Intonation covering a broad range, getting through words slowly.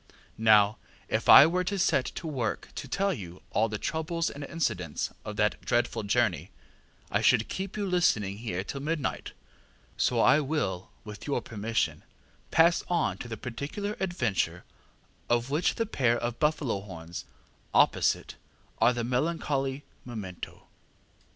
No: wide, 7.3 semitones; average, 145 wpm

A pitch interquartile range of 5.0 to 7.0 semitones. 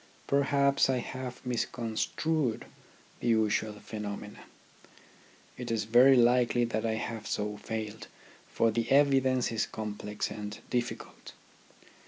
No: average, 2.9 semitones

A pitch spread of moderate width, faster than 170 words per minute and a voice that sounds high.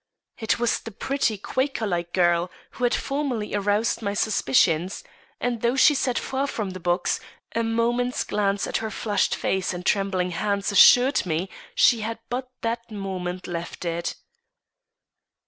No: average, 4.5 semitones; average, 155 wpm; high, 210 Hz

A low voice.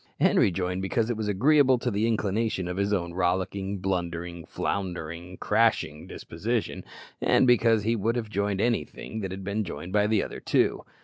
Yes: low, 100 Hz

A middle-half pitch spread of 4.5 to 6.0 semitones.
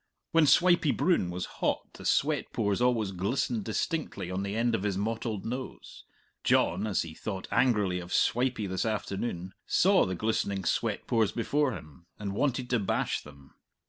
Yes: average, 4.8 semitones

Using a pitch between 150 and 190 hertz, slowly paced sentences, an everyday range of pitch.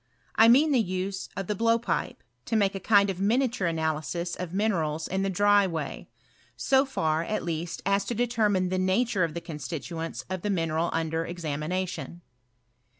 No: medium, 185 Hz; average, 175 wpm; average, 3.9 semitones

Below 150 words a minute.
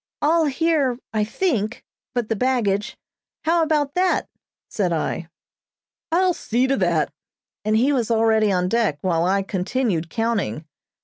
Yes: average, 140 wpm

